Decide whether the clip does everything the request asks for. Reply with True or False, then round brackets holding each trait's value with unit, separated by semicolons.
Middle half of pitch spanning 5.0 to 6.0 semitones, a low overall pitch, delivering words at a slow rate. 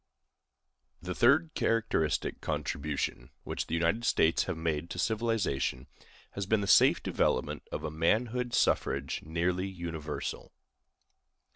True (5.6 semitones; 90 Hz; 120 wpm)